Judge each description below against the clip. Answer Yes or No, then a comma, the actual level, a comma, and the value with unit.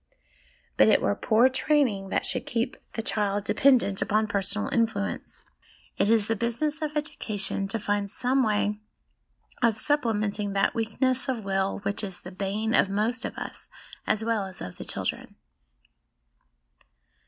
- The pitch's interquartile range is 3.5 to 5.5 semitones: No, average, 3.1 semitones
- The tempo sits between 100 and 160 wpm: Yes, average, 155 wpm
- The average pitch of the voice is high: Yes, high, 215 Hz